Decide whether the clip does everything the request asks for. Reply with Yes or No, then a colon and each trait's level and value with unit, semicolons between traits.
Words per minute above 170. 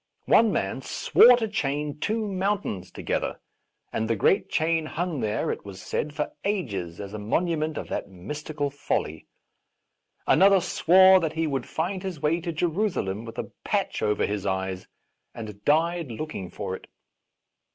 No: average, 160 wpm